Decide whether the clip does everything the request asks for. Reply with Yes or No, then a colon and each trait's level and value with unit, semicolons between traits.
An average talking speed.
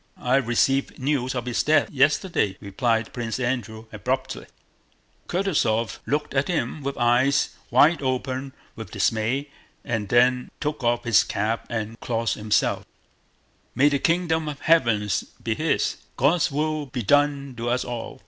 Yes: average, 145 wpm